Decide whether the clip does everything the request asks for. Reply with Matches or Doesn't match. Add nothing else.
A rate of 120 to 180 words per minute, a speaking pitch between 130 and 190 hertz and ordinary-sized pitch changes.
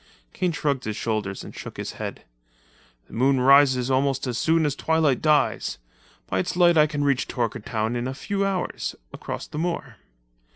Matches